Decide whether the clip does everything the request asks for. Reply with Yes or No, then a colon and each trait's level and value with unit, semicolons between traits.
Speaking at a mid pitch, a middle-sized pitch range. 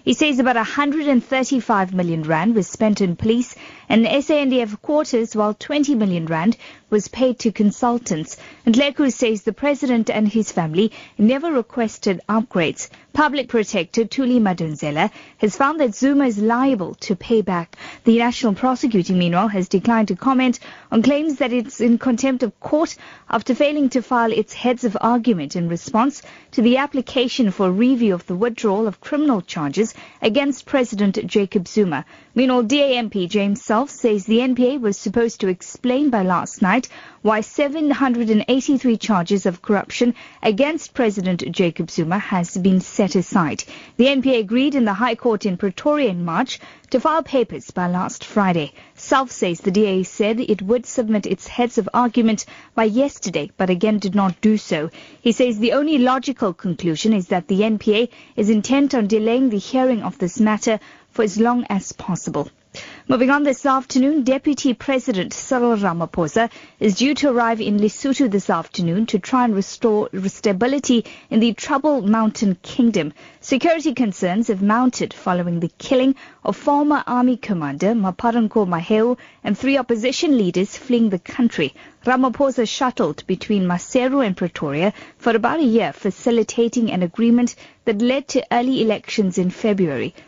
No: high, 230 Hz; average, 4.3 semitones